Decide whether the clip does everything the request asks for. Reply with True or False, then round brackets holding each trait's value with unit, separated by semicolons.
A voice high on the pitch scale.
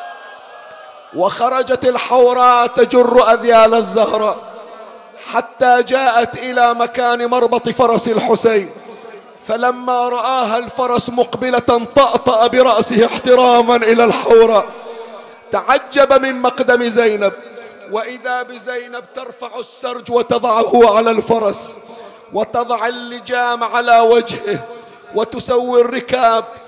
True (235 Hz)